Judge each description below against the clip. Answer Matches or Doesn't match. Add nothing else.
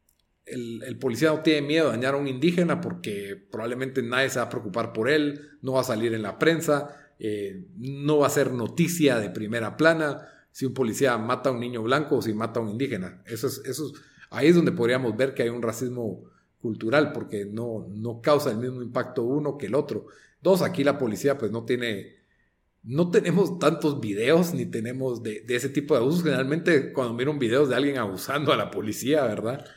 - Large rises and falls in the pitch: Doesn't match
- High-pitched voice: Doesn't match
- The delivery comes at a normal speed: Doesn't match